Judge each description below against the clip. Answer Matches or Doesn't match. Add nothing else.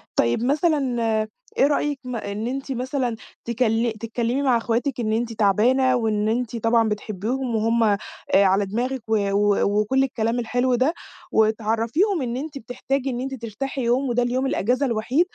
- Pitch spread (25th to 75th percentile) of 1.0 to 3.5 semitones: Matches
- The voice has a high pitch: Matches